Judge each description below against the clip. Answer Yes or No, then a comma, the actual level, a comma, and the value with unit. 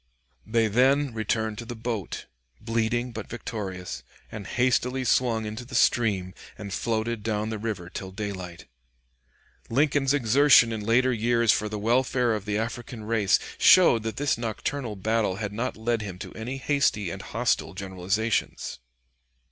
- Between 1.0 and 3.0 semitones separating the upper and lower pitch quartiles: Yes, narrow, 2.6 semitones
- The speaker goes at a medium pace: Yes, average, 150 wpm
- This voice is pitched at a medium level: No, low, 110 Hz